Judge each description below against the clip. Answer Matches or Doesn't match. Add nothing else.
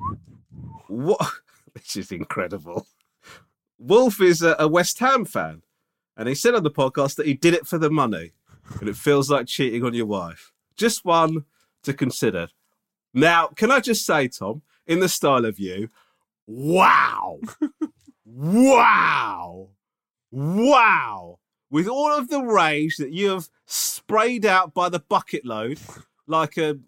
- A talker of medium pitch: Matches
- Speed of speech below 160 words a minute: Matches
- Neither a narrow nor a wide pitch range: Doesn't match